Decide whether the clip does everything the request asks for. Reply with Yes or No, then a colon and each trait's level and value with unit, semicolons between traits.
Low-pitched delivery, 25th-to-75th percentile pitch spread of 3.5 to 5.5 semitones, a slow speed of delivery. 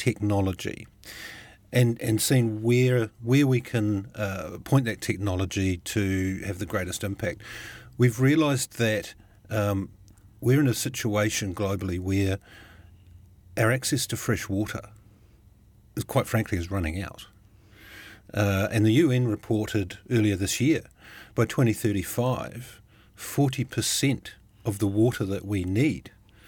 No: low, 105 Hz; average, 3.1 semitones; slow, 125 wpm